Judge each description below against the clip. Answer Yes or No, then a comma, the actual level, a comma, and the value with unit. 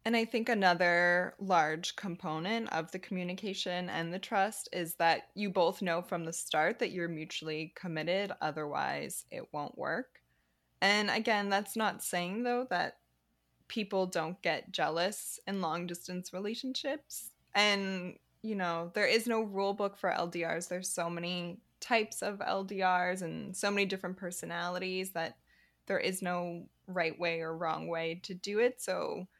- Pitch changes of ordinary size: Yes, average, 3.1 semitones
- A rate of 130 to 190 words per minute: Yes, average, 155 wpm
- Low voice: No, medium, 180 Hz